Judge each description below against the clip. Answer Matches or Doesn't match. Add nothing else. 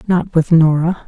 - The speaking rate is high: Doesn't match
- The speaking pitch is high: Doesn't match